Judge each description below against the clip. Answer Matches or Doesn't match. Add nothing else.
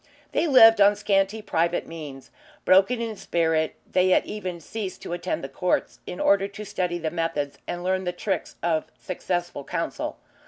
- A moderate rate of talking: Matches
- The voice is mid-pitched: Matches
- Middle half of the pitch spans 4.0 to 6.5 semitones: Doesn't match